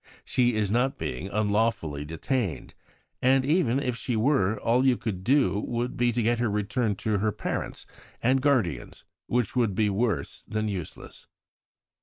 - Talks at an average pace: Yes, average, 160 wpm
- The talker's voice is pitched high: No, low, 115 Hz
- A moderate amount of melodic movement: Yes, average, 3.6 semitones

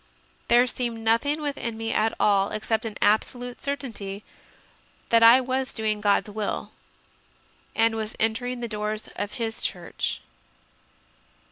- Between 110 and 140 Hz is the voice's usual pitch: No, high, 225 Hz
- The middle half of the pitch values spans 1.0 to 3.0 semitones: Yes, narrow, 2.4 semitones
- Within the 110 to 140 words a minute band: Yes, slow, 135 wpm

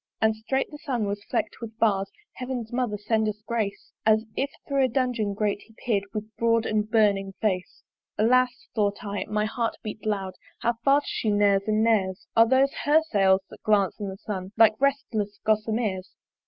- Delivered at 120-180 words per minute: No, average, 190 wpm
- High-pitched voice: Yes, high, 215 Hz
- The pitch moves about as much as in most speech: No, narrow, 2.3 semitones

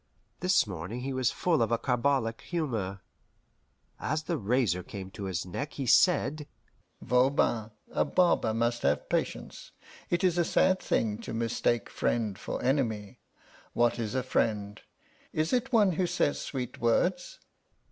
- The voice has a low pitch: Yes, low, 125 Hz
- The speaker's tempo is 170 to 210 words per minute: No, average, 150 wpm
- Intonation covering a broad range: Yes, wide, 6.1 semitones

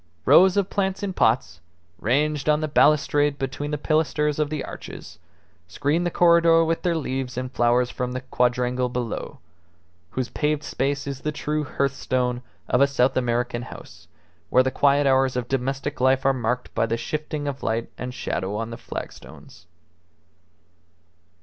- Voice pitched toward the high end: No, low, 135 Hz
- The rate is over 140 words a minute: Yes, average, 160 wpm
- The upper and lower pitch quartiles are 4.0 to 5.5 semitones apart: No, average, 3.3 semitones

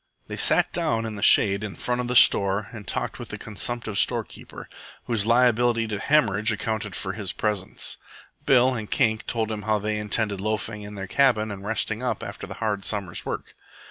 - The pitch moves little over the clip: Yes, narrow, 2.1 semitones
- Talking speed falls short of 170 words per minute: No, average, 195 wpm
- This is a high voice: No, low, 110 Hz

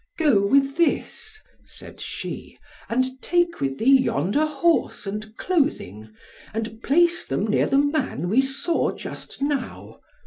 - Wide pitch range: Yes, wide, 6.1 semitones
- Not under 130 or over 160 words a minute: Yes, slow, 135 wpm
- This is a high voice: Yes, very high, 270 Hz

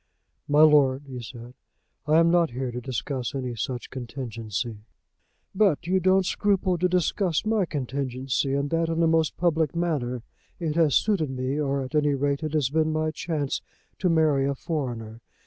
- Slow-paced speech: No, average, 175 wpm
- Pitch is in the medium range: Yes, medium, 145 Hz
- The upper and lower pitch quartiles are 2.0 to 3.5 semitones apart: No, average, 4.2 semitones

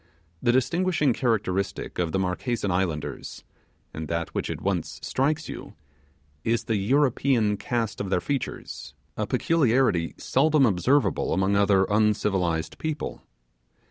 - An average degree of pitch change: No, wide, 5.9 semitones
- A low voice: Yes, low, 105 Hz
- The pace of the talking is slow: Yes, slow, 125 wpm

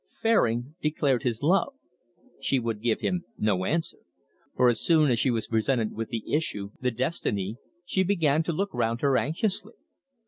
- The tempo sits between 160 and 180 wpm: Yes, average, 170 wpm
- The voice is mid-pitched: No, low, 130 Hz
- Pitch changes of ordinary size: No, wide, 6.3 semitones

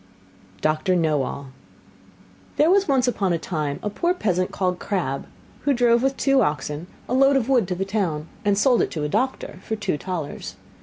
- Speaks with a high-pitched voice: Yes, high, 195 Hz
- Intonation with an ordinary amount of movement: No, wide, 8.3 semitones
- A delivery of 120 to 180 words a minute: No, average, 190 wpm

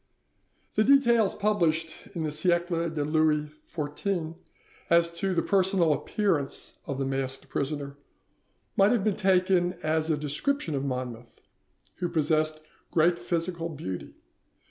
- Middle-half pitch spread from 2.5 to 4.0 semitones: Yes, average, 3.7 semitones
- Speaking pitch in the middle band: Yes, medium, 165 Hz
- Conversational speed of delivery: No, slow, 130 wpm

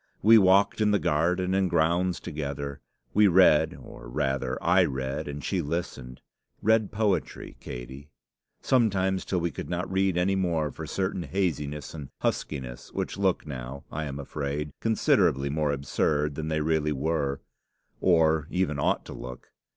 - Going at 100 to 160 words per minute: Yes, average, 155 wpm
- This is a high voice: No, very low, 80 Hz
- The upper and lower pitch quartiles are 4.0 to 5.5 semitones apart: Yes, average, 4.9 semitones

